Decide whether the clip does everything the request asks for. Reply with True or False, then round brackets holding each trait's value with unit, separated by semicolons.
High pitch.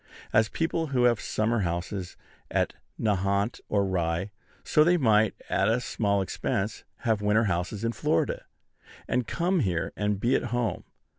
False (105 Hz)